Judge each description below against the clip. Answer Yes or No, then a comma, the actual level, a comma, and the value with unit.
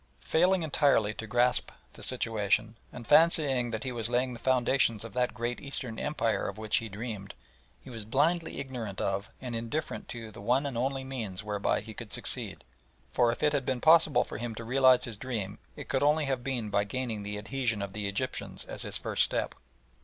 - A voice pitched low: Yes, low, 120 Hz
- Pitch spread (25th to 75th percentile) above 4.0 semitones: No, average, 3.5 semitones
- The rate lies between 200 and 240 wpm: Yes, fast, 205 wpm